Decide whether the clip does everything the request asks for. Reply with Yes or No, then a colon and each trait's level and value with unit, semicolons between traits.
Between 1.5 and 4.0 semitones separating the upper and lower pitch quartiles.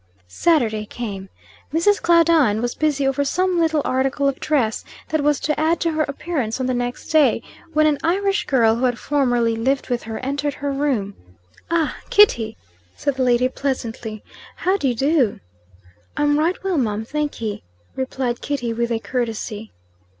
No: average, 4.5 semitones